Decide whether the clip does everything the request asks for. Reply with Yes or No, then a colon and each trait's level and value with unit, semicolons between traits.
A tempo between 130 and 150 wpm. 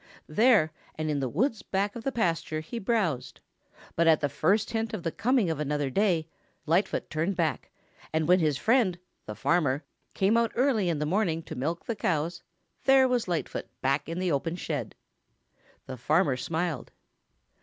No: average, 175 wpm